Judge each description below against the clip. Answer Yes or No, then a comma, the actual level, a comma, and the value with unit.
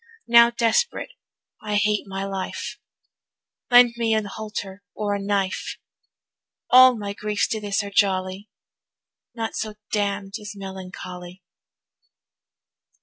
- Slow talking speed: Yes, slow, 115 wpm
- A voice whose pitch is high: Yes, high, 205 Hz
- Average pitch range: No, narrow, 2.0 semitones